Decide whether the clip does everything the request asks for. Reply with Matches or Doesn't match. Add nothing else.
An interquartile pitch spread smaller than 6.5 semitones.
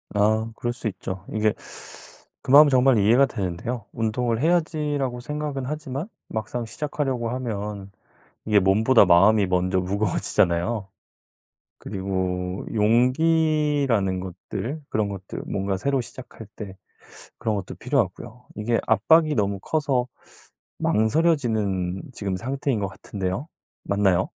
Matches